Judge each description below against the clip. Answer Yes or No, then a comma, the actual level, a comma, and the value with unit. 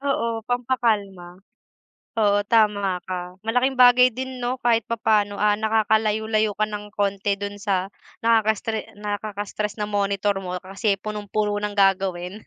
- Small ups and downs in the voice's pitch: Yes, narrow, 1.9 semitones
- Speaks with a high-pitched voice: Yes, high, 210 Hz